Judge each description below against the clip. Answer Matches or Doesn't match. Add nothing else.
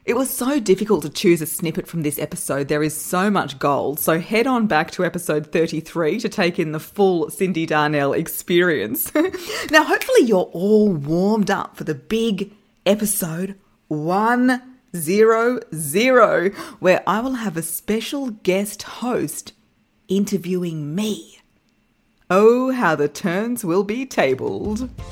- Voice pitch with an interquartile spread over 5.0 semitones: Matches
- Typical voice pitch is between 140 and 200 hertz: Matches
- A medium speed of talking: Matches